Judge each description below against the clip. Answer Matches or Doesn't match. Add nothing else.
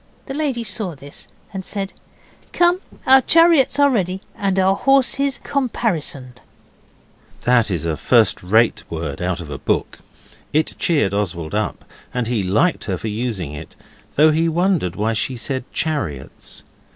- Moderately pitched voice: Matches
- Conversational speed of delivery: Matches